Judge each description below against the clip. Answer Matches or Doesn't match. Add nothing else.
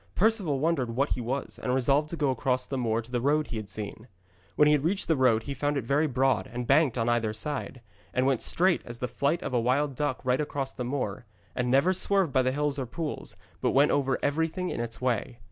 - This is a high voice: Doesn't match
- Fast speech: Matches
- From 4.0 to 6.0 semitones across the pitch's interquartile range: Doesn't match